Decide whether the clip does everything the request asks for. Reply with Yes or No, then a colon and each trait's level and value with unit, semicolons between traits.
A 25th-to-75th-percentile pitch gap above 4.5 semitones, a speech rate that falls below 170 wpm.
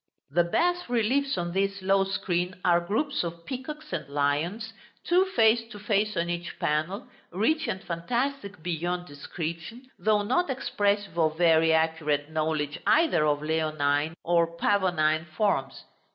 Yes: wide, 5.4 semitones; average, 140 wpm